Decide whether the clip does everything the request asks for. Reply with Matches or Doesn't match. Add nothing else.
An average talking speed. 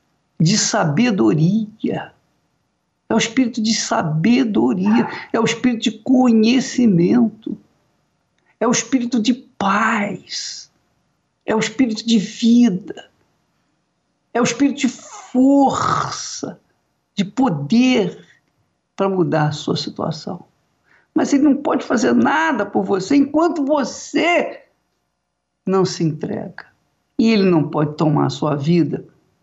Doesn't match